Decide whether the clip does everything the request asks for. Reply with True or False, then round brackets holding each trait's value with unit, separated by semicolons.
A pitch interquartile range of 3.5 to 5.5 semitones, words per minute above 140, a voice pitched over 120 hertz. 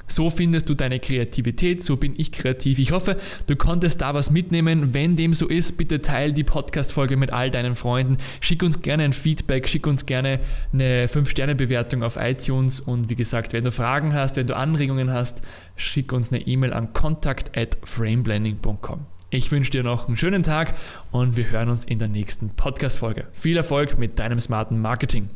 True (3.9 semitones; 190 wpm; 135 Hz)